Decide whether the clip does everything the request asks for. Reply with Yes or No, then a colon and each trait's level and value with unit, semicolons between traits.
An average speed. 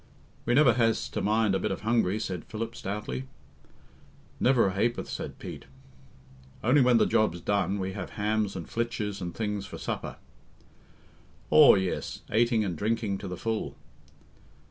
Yes: average, 160 wpm